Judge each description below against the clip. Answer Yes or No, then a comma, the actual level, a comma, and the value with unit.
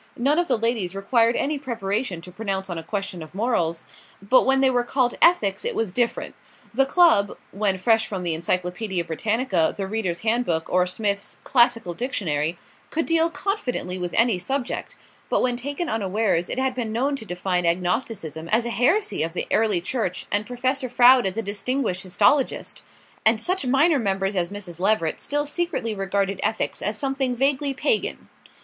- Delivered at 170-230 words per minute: Yes, average, 175 wpm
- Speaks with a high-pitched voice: Yes, high, 220 Hz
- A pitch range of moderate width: No, wide, 5.7 semitones